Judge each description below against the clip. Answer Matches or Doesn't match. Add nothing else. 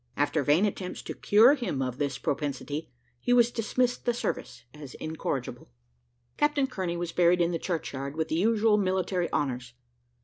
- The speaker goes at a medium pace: Matches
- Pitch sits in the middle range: Matches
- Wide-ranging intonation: Matches